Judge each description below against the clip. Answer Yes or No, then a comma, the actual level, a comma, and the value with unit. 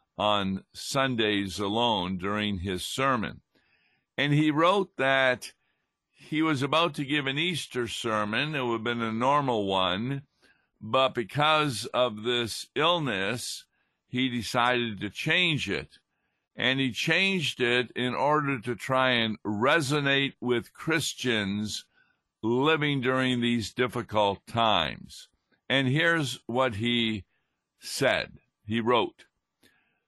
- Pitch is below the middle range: Yes, low, 125 Hz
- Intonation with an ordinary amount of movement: Yes, average, 4.2 semitones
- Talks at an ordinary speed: No, slow, 120 wpm